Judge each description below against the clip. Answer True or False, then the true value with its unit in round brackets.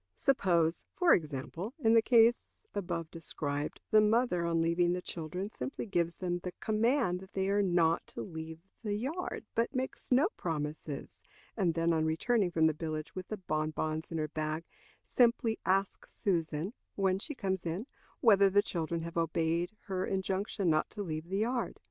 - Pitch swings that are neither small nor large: True (4.6 semitones)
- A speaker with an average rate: True (175 wpm)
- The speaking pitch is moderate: True (180 Hz)